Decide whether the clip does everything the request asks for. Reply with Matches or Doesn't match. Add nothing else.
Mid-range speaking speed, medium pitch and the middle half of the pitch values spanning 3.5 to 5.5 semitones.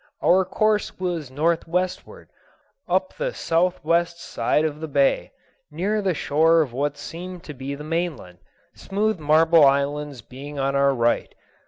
Matches